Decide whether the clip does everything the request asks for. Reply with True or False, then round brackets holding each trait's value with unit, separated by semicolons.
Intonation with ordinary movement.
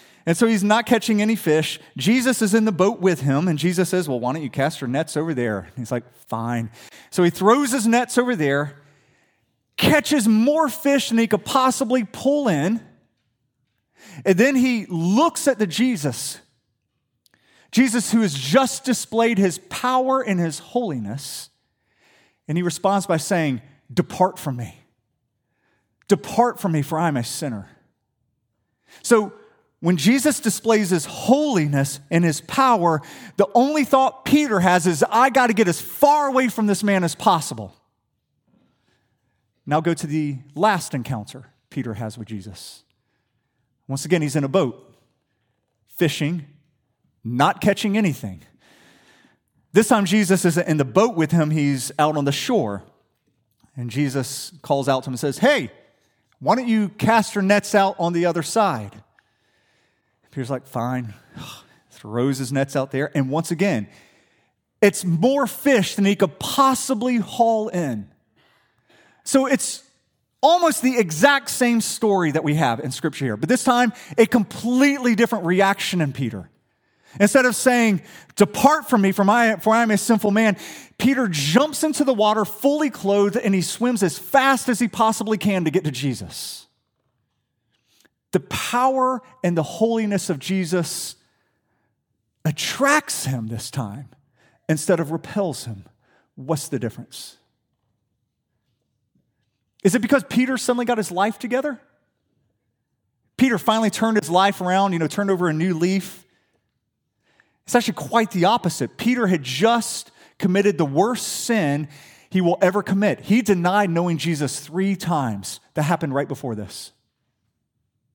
False (8.9 semitones)